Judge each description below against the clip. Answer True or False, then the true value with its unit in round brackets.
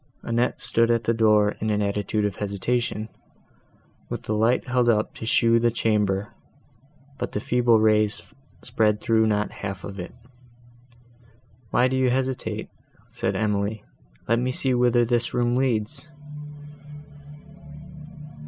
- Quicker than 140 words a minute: False (135 wpm)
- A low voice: True (115 Hz)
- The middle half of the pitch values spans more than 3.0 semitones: False (2.5 semitones)